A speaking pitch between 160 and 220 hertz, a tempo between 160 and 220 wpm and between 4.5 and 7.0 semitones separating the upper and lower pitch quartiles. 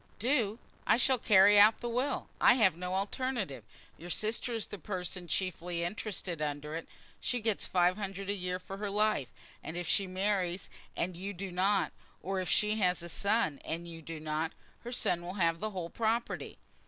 No: high, 190 Hz; average, 185 wpm; average, 3.5 semitones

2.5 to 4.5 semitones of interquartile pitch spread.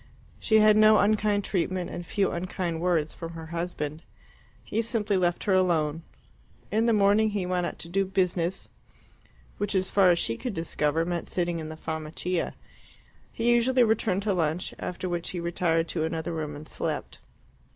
Yes: average, 3.6 semitones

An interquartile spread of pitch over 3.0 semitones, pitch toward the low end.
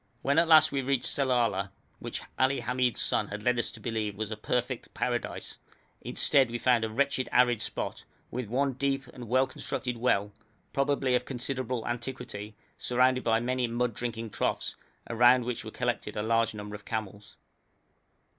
No: narrow, 2.4 semitones; low, 125 Hz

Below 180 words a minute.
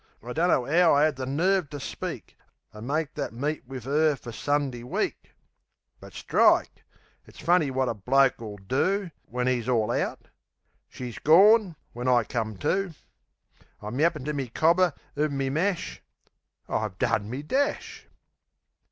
Yes: average, 145 wpm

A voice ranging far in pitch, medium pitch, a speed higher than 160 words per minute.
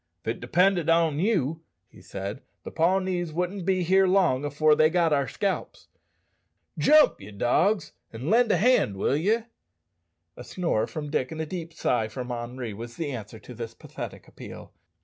Yes: wide, 6.8 semitones; medium, 160 Hz; average, 170 wpm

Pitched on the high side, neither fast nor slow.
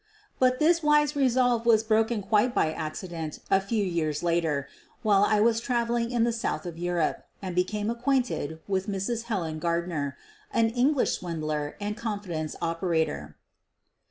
Yes: high, 200 Hz; average, 155 wpm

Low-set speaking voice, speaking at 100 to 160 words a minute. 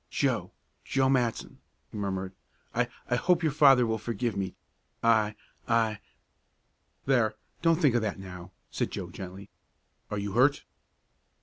Yes: low, 115 Hz; average, 145 wpm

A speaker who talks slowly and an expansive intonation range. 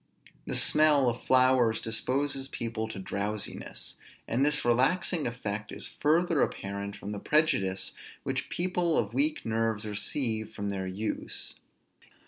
Yes: slow, 130 wpm; wide, 5.7 semitones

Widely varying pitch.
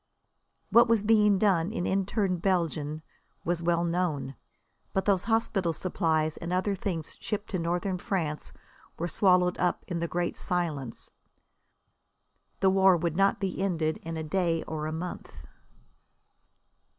No: average, 2.8 semitones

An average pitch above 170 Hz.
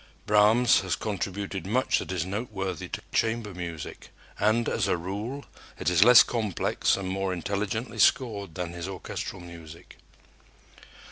No: low, 100 Hz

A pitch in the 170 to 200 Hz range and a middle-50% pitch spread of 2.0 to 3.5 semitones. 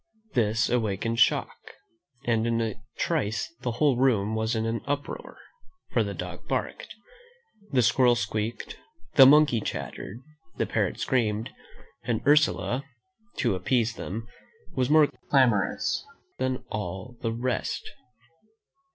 No: low, 115 Hz; average, 2.8 semitones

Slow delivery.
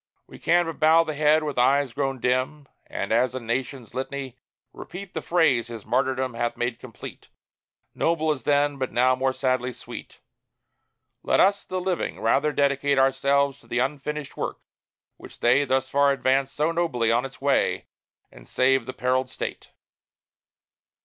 No: average, 165 wpm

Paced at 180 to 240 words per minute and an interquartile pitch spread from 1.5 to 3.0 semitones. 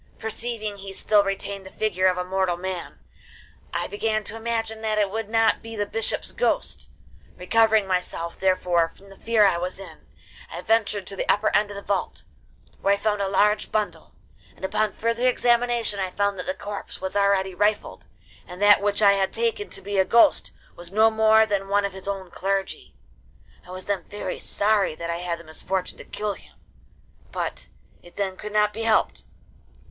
Yes: average, 195 wpm; narrow, 2.4 semitones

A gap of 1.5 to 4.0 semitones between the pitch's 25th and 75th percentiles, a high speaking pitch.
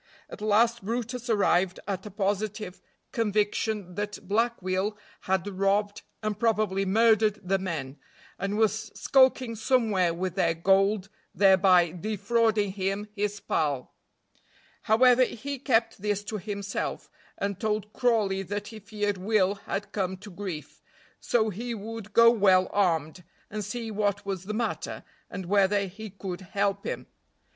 Yes: narrow, 2.4 semitones; high, 205 Hz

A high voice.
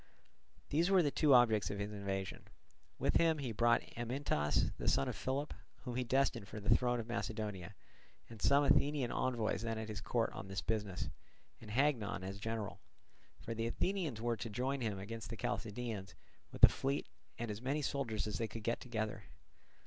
No: low, 115 Hz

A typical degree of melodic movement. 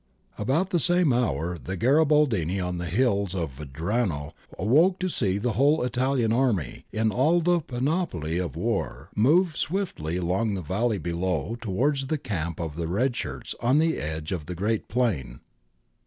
No: wide, 8.0 semitones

